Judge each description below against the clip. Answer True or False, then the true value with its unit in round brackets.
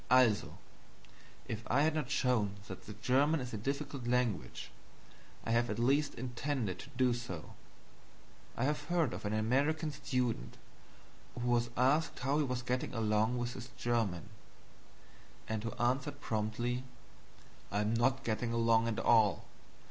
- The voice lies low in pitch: True (120 Hz)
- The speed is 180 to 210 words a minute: False (150 wpm)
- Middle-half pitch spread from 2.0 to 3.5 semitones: True (3.2 semitones)